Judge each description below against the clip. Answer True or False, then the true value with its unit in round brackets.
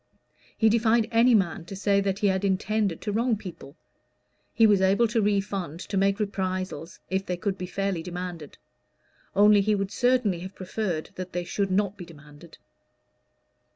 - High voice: True (195 Hz)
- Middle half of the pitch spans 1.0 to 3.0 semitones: True (2.5 semitones)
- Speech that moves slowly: False (170 wpm)